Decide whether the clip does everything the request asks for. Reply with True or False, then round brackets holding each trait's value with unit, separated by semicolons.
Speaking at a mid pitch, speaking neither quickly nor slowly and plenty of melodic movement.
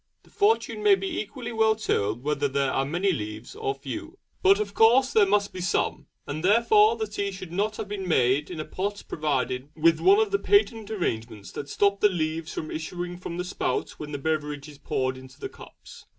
False (180 Hz; 210 wpm; 7.1 semitones)